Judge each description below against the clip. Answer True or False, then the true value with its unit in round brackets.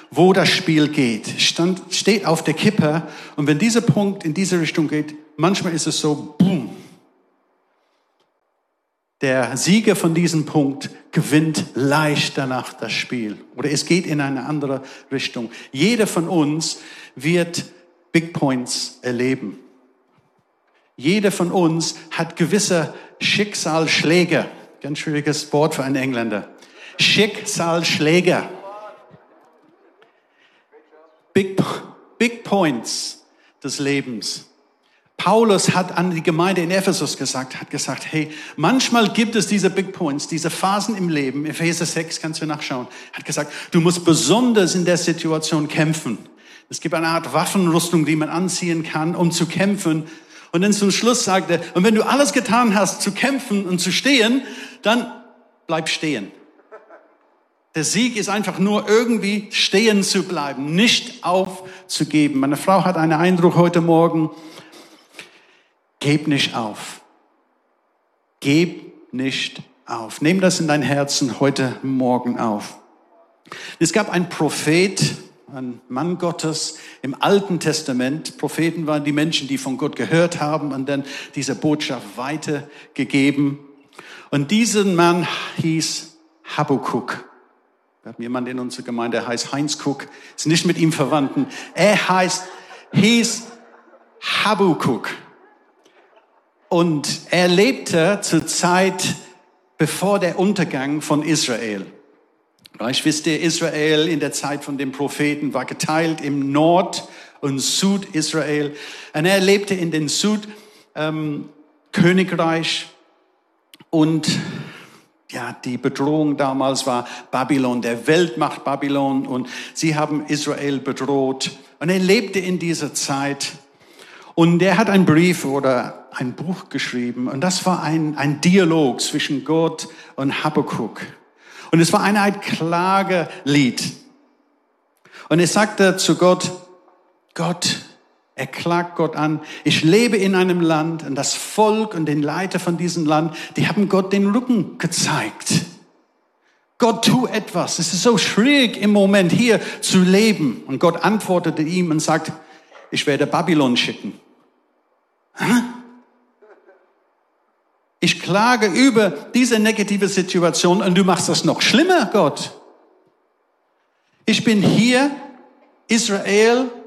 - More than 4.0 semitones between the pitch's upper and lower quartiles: True (4.4 semitones)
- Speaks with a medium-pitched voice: True (165 Hz)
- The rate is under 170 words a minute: True (130 wpm)